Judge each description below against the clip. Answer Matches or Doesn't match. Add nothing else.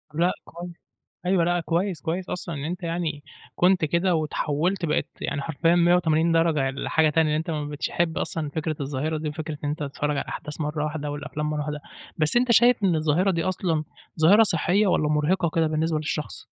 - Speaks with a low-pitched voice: Doesn't match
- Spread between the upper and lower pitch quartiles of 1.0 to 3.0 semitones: Matches